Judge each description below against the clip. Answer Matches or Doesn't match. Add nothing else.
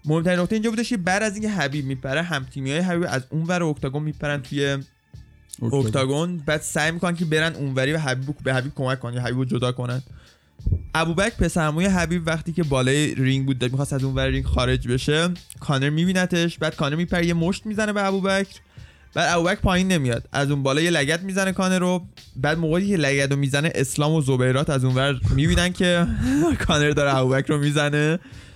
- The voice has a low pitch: Doesn't match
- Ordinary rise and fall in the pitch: Matches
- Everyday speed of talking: Doesn't match